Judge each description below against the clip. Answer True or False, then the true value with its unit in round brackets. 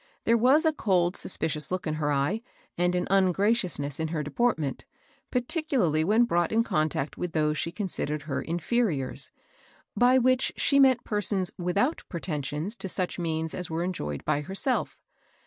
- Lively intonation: True (6.5 semitones)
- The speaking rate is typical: True (160 wpm)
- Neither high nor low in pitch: True (180 Hz)